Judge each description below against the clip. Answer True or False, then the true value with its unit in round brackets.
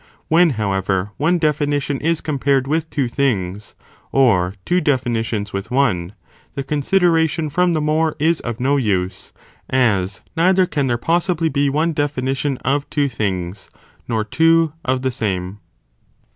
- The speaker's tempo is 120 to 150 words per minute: True (145 wpm)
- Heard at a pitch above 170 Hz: False (135 Hz)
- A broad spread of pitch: True (6.4 semitones)